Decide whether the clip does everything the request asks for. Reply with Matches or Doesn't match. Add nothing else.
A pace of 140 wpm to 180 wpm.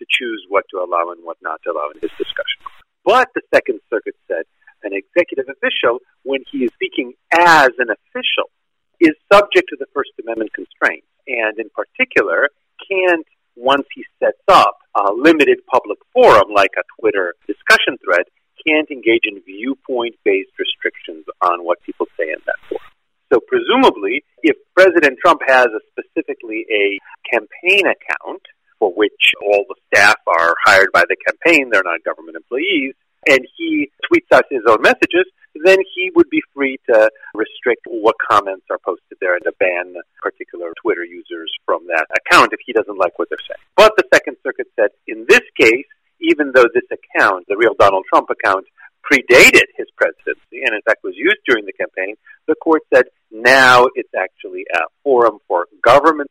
Matches